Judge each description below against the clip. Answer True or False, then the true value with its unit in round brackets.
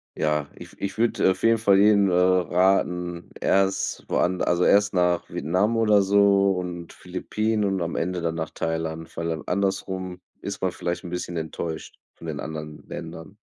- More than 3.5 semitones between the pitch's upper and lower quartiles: False (2.8 semitones)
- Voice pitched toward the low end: True (90 Hz)